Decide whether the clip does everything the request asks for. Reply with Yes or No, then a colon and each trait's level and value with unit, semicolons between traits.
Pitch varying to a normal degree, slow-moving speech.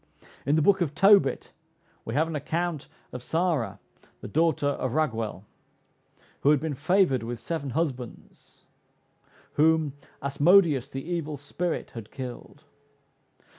Yes: average, 3.9 semitones; slow, 130 wpm